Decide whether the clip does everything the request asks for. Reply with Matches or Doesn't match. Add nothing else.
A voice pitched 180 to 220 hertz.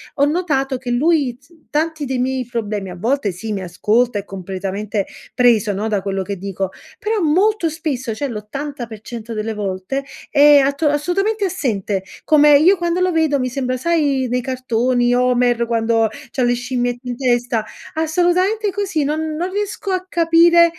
Doesn't match